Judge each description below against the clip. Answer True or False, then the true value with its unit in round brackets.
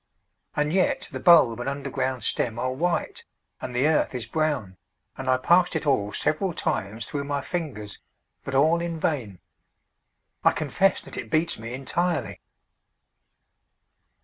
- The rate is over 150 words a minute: False (145 wpm)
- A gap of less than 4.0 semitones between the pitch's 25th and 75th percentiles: False (4.7 semitones)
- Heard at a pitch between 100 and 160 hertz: True (140 Hz)